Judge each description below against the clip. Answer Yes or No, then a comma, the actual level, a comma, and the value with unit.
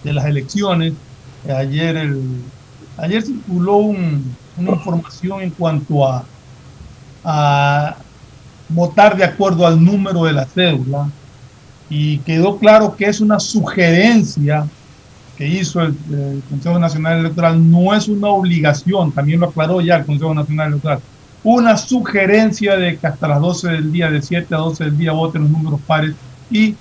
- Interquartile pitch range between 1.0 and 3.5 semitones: No, average, 4.2 semitones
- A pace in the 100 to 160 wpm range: Yes, average, 155 wpm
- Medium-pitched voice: Yes, medium, 160 Hz